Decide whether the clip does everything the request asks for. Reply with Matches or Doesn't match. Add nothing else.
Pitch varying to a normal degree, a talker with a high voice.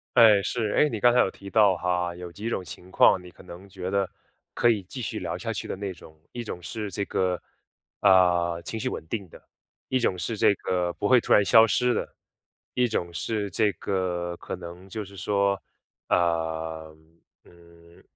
Doesn't match